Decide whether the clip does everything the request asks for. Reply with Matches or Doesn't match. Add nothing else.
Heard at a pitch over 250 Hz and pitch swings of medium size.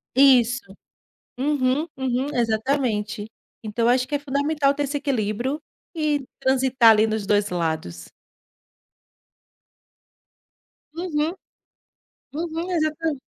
Matches